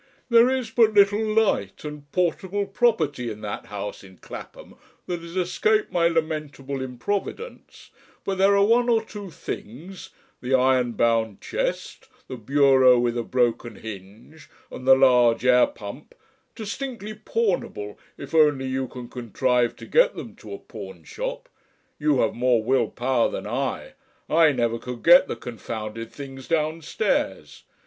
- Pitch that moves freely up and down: Yes, wide, 8.6 semitones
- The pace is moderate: Yes, average, 150 wpm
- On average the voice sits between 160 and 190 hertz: No, medium, 140 Hz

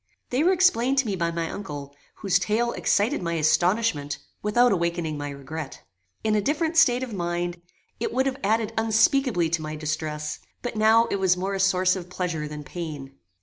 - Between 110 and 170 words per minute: No, average, 190 wpm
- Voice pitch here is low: No, medium, 185 Hz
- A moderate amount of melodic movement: No, wide, 6.1 semitones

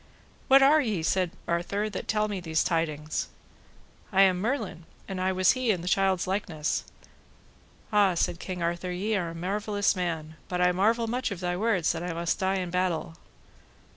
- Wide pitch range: No, average, 3.2 semitones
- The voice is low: No, medium, 185 Hz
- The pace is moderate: Yes, average, 185 wpm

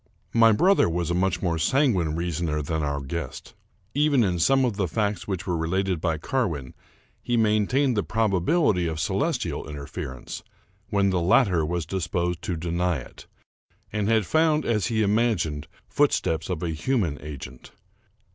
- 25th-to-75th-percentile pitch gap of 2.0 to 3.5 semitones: No, average, 5.3 semitones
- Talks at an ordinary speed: Yes, average, 160 wpm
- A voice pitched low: Yes, very low, 90 Hz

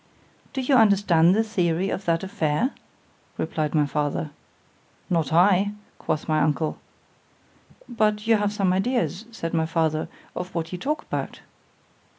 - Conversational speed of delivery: Yes, average, 145 wpm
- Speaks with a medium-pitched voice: Yes, medium, 180 Hz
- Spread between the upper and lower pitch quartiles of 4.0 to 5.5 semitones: Yes, average, 4.7 semitones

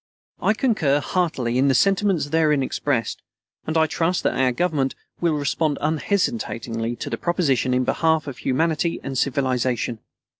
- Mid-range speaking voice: Yes, medium, 145 Hz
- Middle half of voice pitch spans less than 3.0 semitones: No, average, 4.3 semitones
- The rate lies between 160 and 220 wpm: No, average, 150 wpm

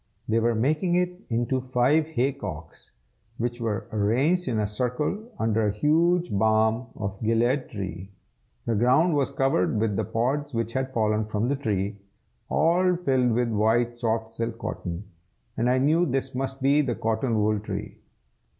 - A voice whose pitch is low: Yes, low, 120 Hz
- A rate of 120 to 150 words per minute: No, average, 165 wpm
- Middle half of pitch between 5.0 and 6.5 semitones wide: No, average, 4.1 semitones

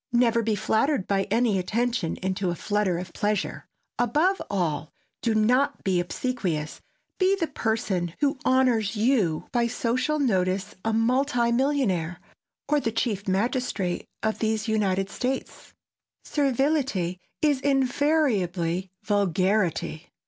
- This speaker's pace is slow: Yes, slow, 120 wpm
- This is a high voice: Yes, high, 220 Hz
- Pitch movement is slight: No, average, 5.3 semitones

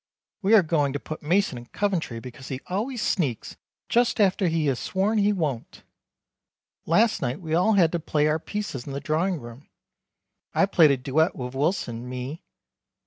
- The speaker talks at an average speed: Yes, average, 180 wpm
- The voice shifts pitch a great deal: Yes, wide, 6.5 semitones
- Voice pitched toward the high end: No, medium, 160 Hz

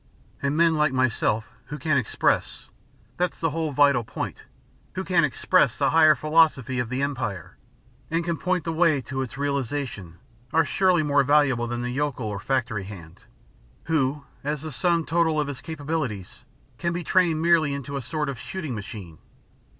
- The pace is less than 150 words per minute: No, average, 175 wpm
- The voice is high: No, medium, 145 Hz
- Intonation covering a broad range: No, average, 4.5 semitones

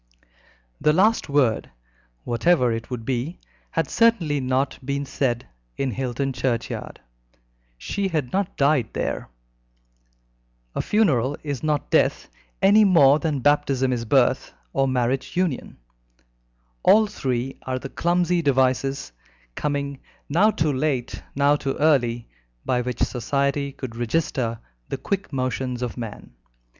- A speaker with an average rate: No, slow, 130 wpm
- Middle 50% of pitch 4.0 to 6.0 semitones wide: No, average, 3.6 semitones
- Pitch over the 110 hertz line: Yes, low, 135 Hz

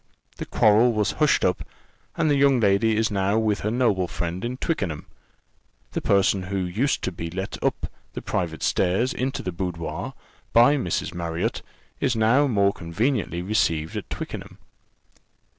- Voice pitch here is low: Yes, low, 100 Hz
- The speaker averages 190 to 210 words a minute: No, average, 160 wpm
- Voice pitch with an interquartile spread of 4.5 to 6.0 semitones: Yes, average, 4.9 semitones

